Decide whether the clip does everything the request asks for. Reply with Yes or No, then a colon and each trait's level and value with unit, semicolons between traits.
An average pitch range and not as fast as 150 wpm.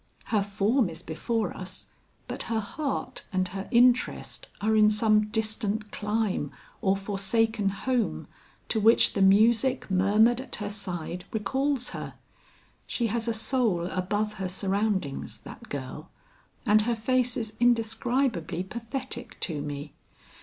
Yes: average, 3.3 semitones; slow, 135 wpm